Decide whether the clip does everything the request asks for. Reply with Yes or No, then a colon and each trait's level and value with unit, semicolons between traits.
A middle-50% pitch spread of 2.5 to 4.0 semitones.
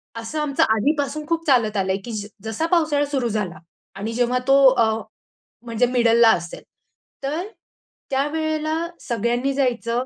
No: average, 4.4 semitones